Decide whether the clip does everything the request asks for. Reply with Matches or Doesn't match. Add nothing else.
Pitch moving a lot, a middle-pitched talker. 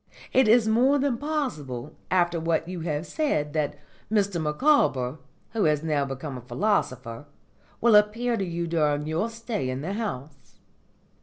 Matches